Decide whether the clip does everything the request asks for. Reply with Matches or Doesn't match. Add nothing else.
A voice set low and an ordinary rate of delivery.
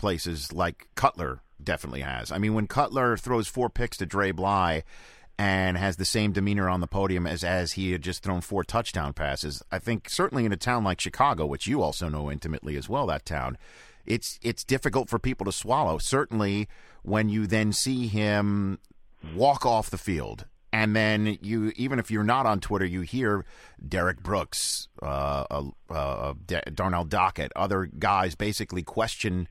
Matches